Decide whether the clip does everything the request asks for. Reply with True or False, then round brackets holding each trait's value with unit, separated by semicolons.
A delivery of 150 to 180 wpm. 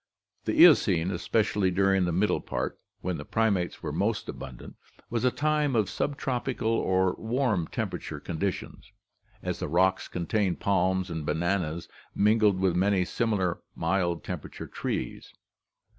False (135 wpm)